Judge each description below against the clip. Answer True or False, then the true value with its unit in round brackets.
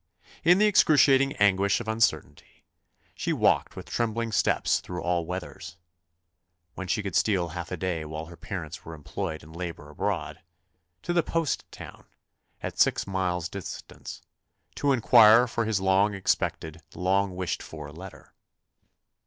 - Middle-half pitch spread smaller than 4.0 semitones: False (4.6 semitones)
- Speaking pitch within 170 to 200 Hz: False (95 Hz)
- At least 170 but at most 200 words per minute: False (145 wpm)